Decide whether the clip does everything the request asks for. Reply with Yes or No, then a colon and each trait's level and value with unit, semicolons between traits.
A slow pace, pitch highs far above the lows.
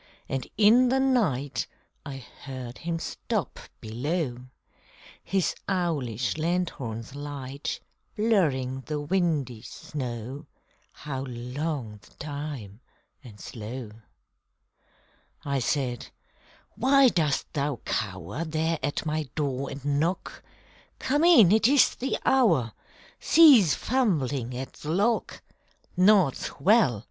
Yes: slow, 105 wpm; wide, 6.3 semitones